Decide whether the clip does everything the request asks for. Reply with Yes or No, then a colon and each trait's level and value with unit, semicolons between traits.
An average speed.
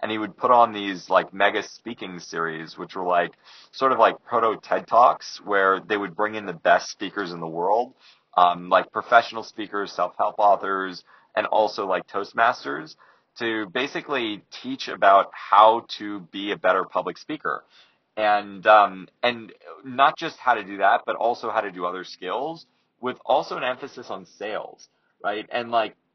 Yes: average, 175 wpm